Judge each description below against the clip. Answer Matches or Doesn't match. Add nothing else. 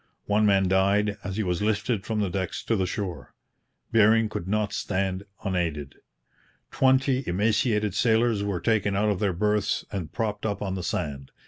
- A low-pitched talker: Matches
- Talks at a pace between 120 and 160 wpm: Doesn't match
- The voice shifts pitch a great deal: Doesn't match